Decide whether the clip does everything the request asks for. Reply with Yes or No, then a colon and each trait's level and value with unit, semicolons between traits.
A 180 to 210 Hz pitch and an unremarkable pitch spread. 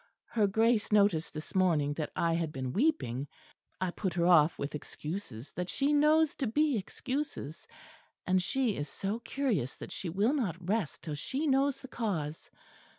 No: high, 190 Hz; wide, 8.5 semitones